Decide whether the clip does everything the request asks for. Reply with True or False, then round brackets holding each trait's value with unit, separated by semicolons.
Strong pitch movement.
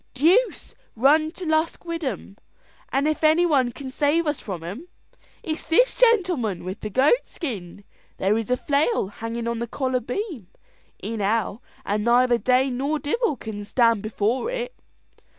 True (6.0 semitones)